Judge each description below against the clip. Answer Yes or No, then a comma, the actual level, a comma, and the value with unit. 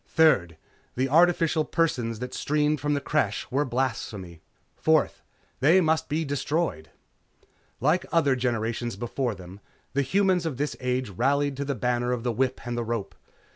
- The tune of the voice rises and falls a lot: No, average, 4.4 semitones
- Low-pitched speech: Yes, low, 130 Hz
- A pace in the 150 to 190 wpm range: Yes, average, 160 wpm